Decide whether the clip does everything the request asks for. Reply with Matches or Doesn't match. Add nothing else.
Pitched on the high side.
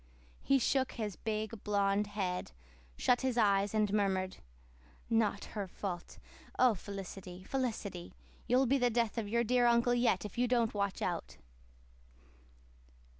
Matches